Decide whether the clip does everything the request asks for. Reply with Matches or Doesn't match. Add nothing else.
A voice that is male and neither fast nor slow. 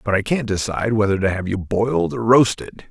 Doesn't match